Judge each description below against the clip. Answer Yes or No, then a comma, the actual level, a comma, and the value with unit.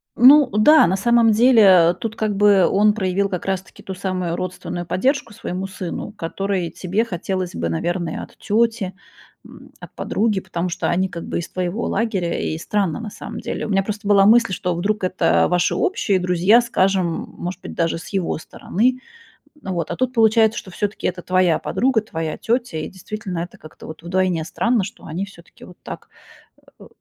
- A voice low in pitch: No, high, 190 Hz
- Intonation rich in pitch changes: No, average, 3.5 semitones